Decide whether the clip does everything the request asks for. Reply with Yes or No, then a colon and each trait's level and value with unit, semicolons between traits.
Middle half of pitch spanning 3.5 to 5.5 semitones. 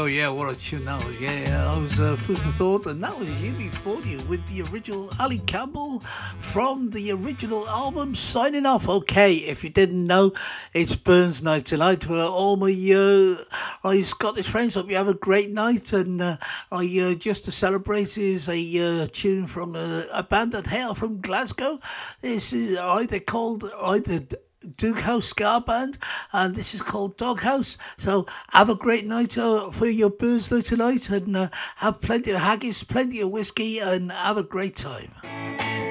Yes: average, 3.8 semitones